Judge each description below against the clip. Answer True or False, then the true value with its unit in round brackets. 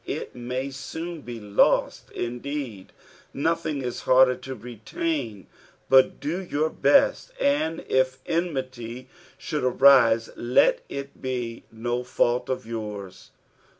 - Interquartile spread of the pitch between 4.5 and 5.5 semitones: False (3.5 semitones)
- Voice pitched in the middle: False (130 Hz)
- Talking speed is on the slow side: True (115 wpm)